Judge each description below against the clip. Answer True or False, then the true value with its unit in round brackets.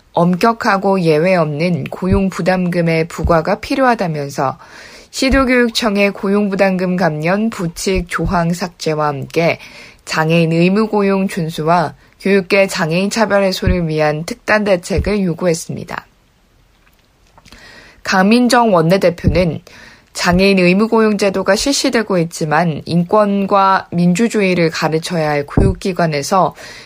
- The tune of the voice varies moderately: True (3.4 semitones)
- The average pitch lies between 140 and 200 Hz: True (185 Hz)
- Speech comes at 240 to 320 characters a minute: True (275 characters per minute)